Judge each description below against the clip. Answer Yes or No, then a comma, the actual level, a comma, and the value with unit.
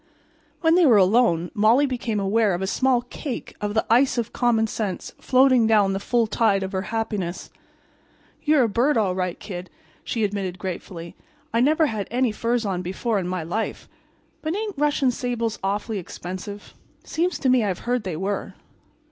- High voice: Yes, high, 220 Hz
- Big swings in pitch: No, average, 4.4 semitones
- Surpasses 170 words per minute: Yes, average, 180 wpm